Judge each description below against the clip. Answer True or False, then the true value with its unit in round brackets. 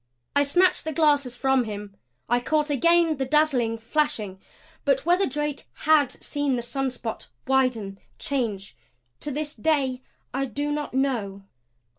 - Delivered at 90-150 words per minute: True (140 wpm)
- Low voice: False (270 Hz)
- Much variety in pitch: False (3.7 semitones)